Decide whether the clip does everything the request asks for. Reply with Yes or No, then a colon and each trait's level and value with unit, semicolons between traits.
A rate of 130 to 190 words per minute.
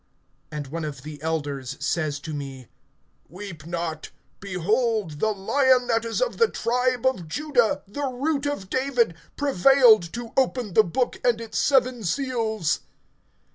Yes: average, 145 wpm